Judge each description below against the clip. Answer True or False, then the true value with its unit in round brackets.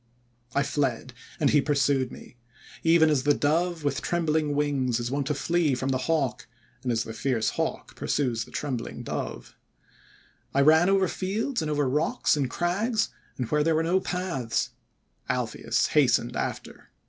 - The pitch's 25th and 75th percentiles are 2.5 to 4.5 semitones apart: True (3.9 semitones)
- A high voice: False (145 Hz)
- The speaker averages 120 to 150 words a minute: False (165 wpm)